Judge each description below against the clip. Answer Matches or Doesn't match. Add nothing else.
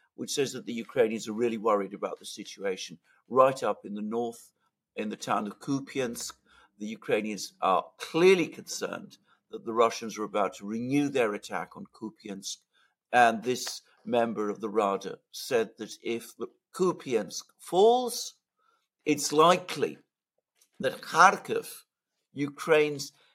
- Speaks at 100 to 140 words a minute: Matches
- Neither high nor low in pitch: Doesn't match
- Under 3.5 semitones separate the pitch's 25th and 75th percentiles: Doesn't match